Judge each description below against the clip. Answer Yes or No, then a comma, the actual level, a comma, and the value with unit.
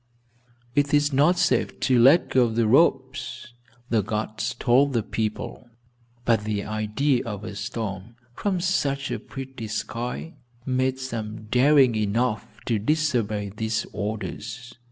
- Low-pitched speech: Yes, low, 120 Hz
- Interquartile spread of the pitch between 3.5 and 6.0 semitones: Yes, average, 3.8 semitones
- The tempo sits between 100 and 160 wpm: Yes, slow, 135 wpm